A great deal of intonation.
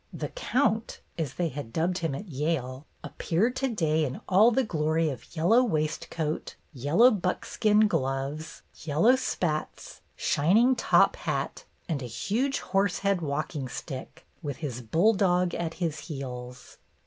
Yes: wide, 6.1 semitones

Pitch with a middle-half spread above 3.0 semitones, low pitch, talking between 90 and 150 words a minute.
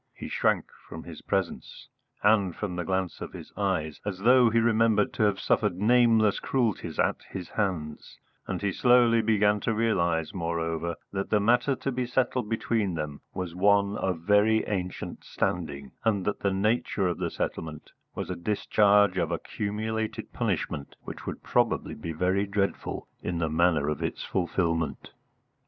No: average, 4.3 semitones; low, 100 Hz; average, 165 wpm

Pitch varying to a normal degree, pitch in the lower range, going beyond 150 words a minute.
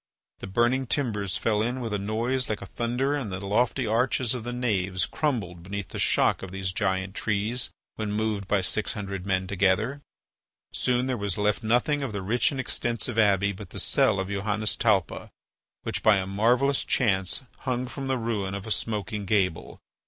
Yes: average, 3.8 semitones; low, 105 Hz; average, 185 wpm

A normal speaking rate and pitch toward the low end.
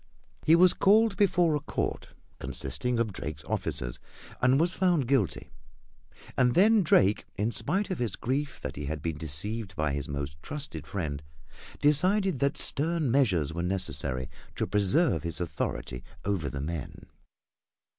Yes: average, 150 wpm; low, 105 Hz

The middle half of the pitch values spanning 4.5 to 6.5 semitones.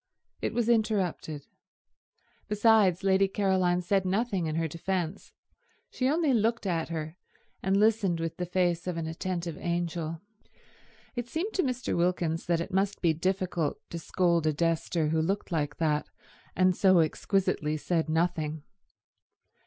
No: average, 3.2 semitones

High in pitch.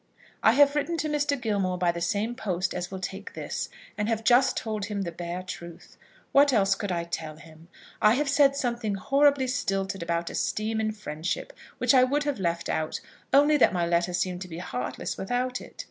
Yes: high, 205 Hz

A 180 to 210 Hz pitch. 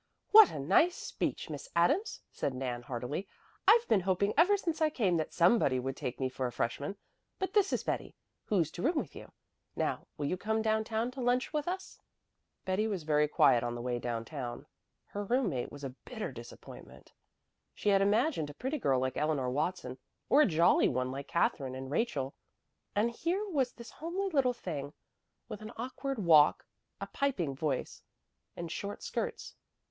Yes: medium, 185 Hz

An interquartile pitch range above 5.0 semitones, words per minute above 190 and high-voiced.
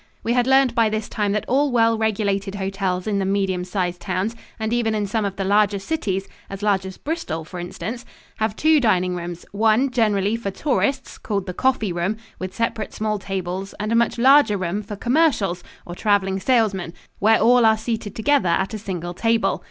No: average, 3.2 semitones; average, 200 wpm; high, 210 Hz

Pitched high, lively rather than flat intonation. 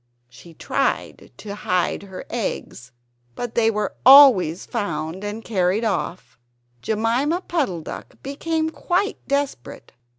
Yes: high, 220 Hz; wide, 7.3 semitones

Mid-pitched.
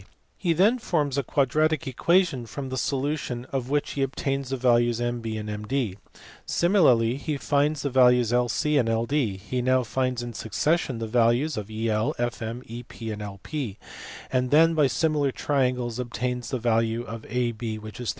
No: low, 125 Hz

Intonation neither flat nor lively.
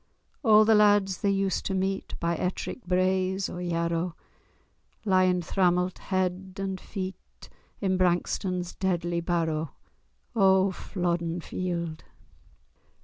No: narrow, 1.7 semitones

